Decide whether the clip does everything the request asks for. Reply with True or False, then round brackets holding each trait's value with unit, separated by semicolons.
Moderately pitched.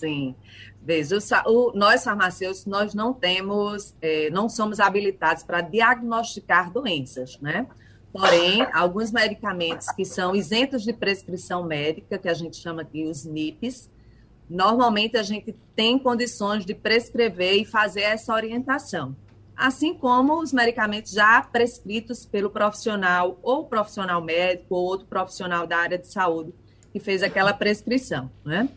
False (205 Hz)